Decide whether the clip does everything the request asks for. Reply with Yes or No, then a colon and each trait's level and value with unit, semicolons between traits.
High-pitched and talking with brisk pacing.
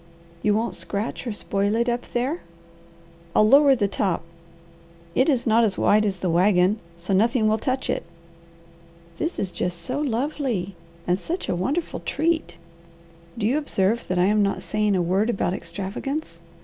No: high, 215 Hz; average, 165 wpm